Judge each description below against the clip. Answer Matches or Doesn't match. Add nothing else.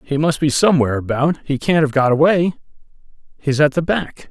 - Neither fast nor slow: Matches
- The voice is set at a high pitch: Doesn't match